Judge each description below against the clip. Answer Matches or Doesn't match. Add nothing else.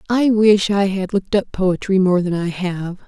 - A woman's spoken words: Matches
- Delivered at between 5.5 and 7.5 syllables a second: Doesn't match